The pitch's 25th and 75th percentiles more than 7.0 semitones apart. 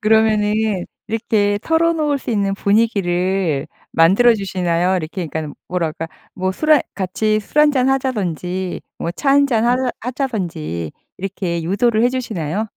No: average, 5.2 semitones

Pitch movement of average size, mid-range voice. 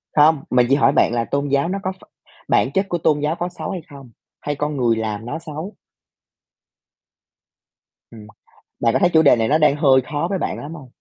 Yes: average, 3.9 semitones; medium, 145 Hz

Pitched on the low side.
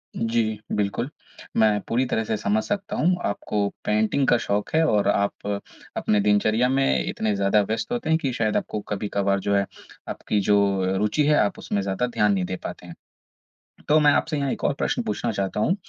Yes: low, 105 Hz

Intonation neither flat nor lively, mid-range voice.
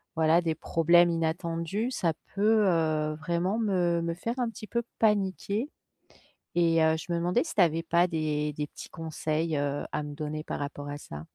Yes: average, 3.3 semitones; medium, 165 Hz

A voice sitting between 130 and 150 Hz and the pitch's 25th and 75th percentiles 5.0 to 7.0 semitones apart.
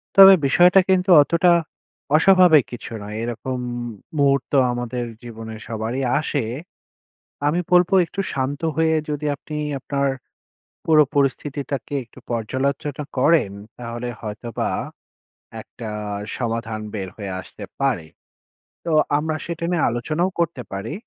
Yes: low, 135 Hz; wide, 5.4 semitones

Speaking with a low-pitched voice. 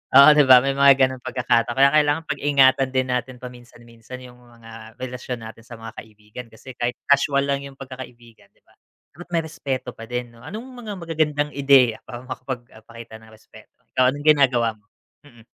Yes: low, 125 Hz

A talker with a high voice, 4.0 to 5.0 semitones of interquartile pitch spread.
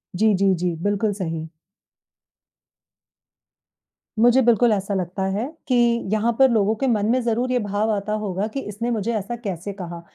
No: high, 210 Hz; average, 3.3 semitones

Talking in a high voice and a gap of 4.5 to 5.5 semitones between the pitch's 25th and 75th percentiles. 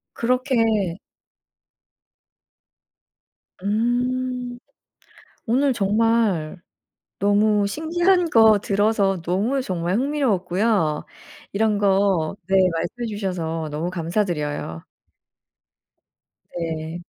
Yes: high, 205 Hz; average, 5.2 semitones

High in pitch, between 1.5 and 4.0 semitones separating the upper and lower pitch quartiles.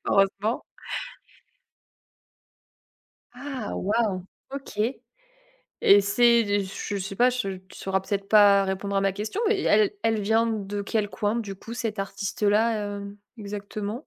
Yes: high, 205 Hz; narrow, 2.4 semitones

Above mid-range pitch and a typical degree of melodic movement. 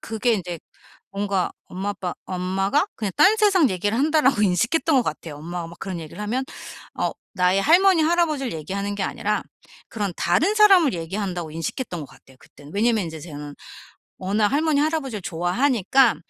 No: high, 205 Hz; wide, 7.7 semitones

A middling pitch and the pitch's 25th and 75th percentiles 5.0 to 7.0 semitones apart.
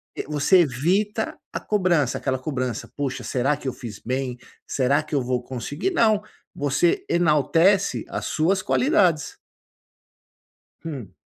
Yes: medium, 145 Hz; wide, 5.5 semitones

